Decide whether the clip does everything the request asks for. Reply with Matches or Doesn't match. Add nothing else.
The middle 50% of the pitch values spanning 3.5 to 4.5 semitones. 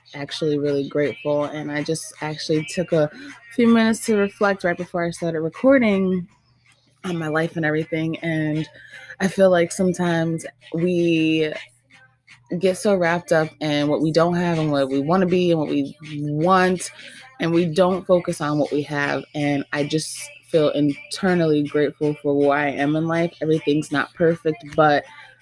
Doesn't match